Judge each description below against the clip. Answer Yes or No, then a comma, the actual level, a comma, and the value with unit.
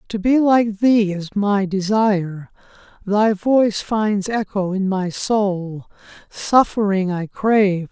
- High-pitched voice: Yes, high, 200 Hz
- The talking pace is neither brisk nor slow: No, slow, 130 wpm